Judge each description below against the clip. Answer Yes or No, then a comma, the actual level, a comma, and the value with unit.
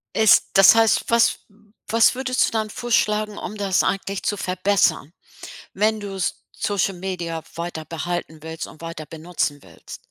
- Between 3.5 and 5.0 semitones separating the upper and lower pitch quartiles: Yes, average, 4.2 semitones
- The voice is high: Yes, high, 195 Hz